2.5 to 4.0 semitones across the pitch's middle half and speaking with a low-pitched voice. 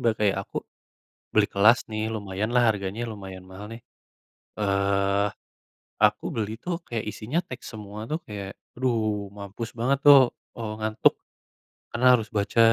Yes: average, 2.9 semitones; low, 105 Hz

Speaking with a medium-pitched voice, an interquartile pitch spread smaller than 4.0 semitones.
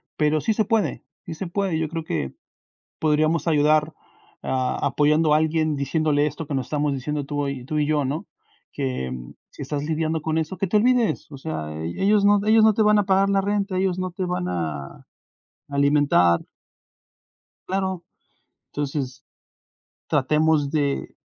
No: medium, 155 Hz; average, 4.6 semitones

